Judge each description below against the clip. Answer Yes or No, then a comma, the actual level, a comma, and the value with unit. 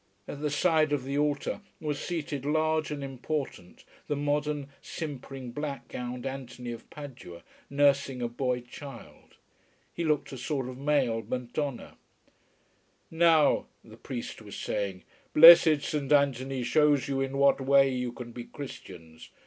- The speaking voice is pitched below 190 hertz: Yes, medium, 140 Hz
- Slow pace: No, average, 145 wpm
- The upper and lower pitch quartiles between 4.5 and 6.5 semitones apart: No, average, 2.9 semitones